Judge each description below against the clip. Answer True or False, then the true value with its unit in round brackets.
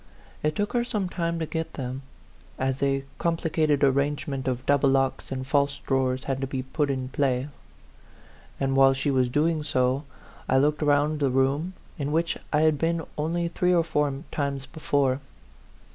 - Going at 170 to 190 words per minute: True (175 wpm)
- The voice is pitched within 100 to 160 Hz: True (140 Hz)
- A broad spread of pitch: False (2.9 semitones)